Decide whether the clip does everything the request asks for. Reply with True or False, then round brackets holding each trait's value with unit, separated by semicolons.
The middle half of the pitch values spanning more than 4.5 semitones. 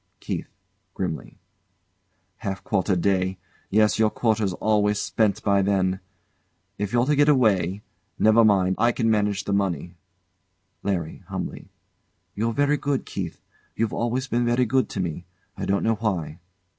False (3.4 semitones)